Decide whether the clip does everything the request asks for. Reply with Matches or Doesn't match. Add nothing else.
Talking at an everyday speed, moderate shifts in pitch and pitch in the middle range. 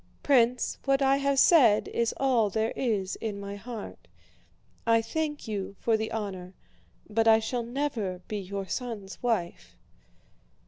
Doesn't match